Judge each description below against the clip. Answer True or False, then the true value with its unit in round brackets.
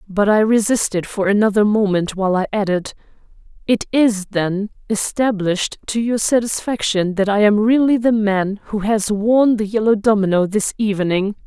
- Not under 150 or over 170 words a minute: True (155 wpm)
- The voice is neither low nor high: False (210 Hz)